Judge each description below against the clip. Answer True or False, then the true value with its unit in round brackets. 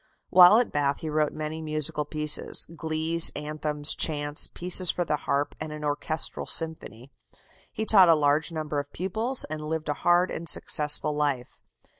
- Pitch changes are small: True (1.9 semitones)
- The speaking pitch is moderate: True (155 Hz)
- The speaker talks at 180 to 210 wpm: False (165 wpm)